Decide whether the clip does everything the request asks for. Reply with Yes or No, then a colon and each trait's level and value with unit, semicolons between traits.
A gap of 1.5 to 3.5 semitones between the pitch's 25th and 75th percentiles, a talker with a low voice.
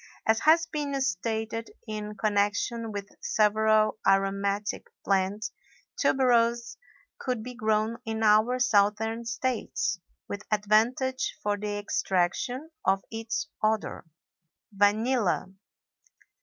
No: narrow, 2.5 semitones; high, 220 Hz